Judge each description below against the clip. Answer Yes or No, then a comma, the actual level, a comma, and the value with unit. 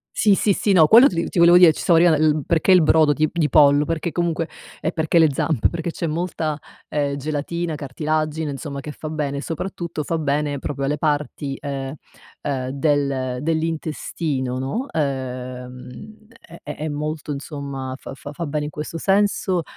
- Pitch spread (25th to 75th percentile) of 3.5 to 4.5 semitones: No, average, 2.7 semitones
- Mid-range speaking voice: Yes, medium, 150 Hz